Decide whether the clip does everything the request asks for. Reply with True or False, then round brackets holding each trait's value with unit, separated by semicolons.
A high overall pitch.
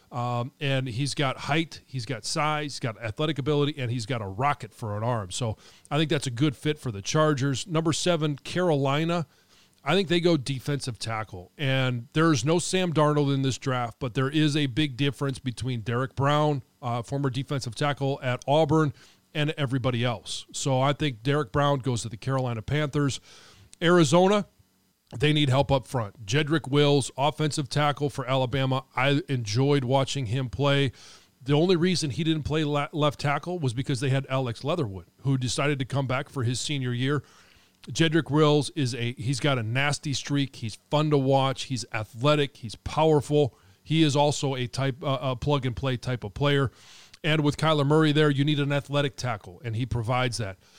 False (140 Hz)